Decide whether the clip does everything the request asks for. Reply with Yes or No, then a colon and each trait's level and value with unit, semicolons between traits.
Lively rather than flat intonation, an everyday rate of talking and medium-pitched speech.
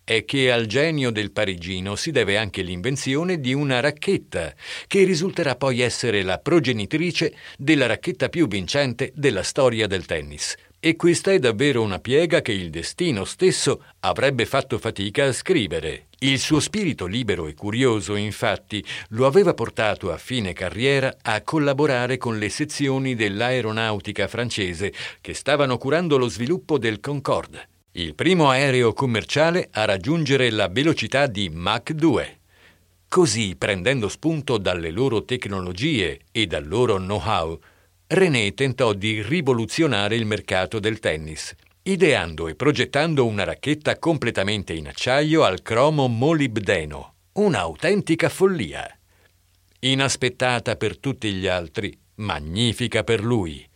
No: wide, 6.3 semitones; average, 135 wpm; low, 120 Hz